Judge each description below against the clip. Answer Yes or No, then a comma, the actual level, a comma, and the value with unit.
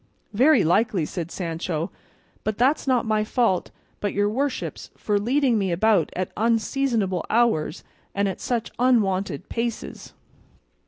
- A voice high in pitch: Yes, high, 215 Hz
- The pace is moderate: No, slow, 130 wpm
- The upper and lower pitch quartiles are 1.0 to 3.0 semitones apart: No, average, 4.3 semitones